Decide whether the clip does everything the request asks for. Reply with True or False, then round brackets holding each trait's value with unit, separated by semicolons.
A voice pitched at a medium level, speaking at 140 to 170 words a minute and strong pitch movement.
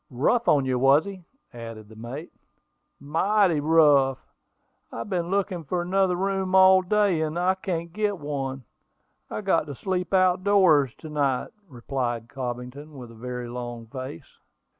True (150 Hz; 160 wpm; 6.5 semitones)